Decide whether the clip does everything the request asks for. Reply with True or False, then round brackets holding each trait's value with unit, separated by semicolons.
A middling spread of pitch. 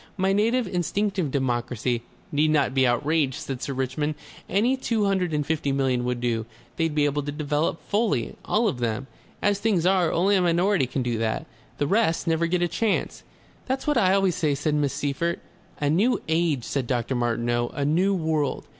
False (6.2 semitones)